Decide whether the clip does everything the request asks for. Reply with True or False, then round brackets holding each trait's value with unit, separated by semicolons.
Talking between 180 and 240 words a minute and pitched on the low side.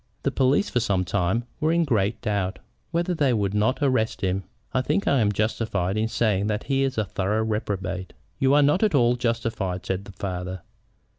True (200 wpm; 110 Hz)